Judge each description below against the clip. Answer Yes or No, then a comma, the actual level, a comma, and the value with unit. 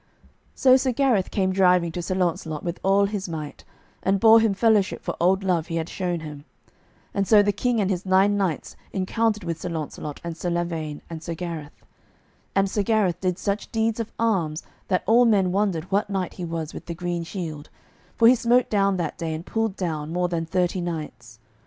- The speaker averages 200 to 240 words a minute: Yes, fast, 205 wpm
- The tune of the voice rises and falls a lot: No, average, 3.5 semitones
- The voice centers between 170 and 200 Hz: Yes, medium, 185 Hz